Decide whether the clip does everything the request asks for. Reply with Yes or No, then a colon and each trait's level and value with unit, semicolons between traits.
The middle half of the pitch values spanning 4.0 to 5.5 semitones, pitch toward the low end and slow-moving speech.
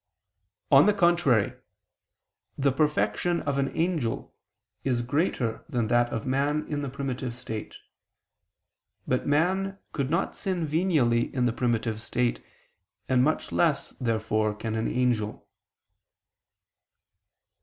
Yes: average, 4.6 semitones; low, 130 Hz; slow, 120 wpm